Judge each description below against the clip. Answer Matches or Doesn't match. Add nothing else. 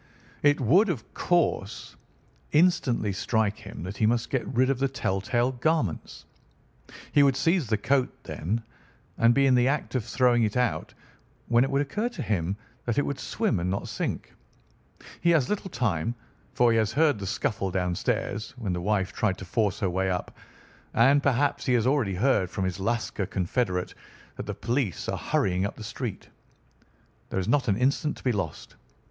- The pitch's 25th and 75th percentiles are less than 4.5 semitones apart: Doesn't match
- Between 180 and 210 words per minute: Matches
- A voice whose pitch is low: Matches